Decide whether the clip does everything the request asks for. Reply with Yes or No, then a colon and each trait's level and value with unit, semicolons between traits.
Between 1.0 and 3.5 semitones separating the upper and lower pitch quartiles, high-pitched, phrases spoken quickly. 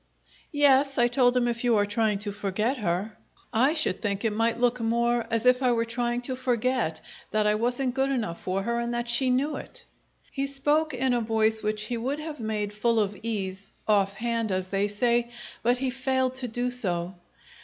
Yes: average, 3.2 semitones; high, 235 Hz; fast, 210 wpm